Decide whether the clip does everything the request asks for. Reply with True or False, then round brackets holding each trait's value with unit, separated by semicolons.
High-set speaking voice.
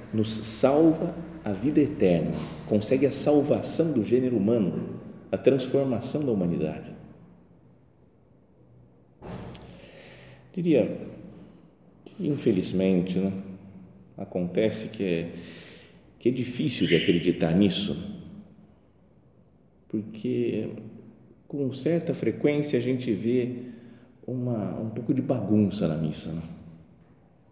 False (120 Hz)